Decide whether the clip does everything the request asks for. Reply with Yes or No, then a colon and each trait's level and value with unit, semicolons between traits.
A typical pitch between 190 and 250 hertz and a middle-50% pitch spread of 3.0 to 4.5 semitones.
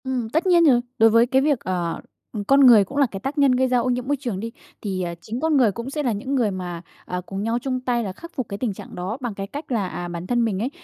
No: high, 235 Hz; average, 5.0 semitones